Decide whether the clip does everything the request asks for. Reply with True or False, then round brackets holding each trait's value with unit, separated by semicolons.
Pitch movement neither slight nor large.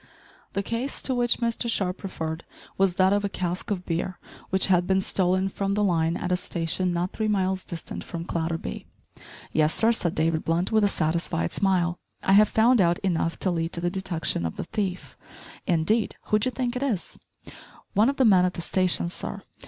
True (3.1 semitones)